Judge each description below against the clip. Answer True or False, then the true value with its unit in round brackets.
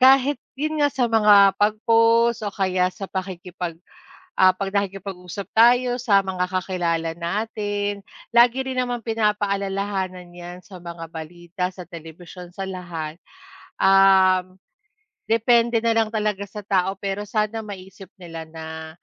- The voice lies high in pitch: True (195 Hz)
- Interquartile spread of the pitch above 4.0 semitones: False (3.6 semitones)